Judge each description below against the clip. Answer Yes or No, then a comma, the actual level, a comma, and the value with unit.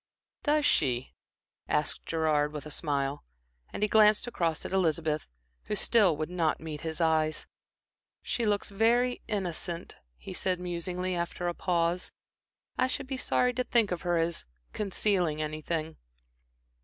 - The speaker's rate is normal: Yes, average, 145 wpm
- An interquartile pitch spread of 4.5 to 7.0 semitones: Yes, average, 4.8 semitones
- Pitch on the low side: No, medium, 175 Hz